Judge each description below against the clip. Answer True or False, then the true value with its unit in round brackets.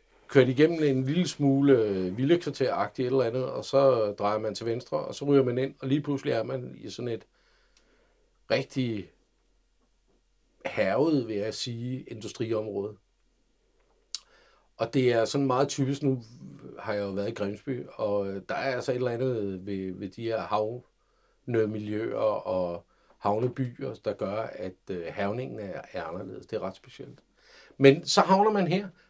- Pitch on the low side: True (125 Hz)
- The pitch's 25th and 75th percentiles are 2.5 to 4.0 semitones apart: False (4.4 semitones)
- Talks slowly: False (160 wpm)